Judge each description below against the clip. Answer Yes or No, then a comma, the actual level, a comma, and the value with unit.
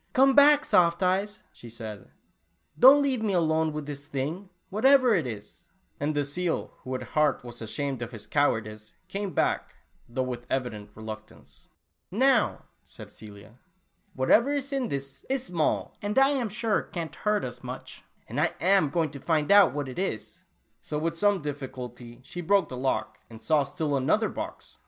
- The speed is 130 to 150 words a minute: No, average, 185 wpm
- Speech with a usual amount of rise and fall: No, wide, 8.2 semitones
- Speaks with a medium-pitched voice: Yes, medium, 155 Hz